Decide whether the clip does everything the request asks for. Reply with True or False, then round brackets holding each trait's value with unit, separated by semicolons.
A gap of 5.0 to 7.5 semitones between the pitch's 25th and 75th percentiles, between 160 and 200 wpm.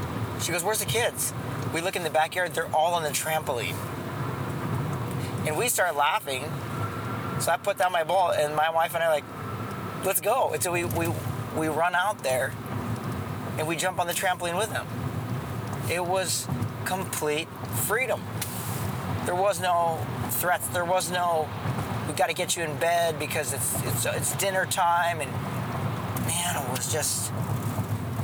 True (5.5 semitones; 170 wpm)